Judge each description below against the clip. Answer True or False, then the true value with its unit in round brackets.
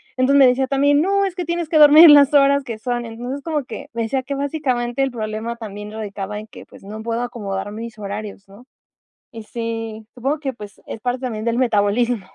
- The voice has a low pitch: False (240 Hz)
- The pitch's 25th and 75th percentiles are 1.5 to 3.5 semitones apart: False (4.3 semitones)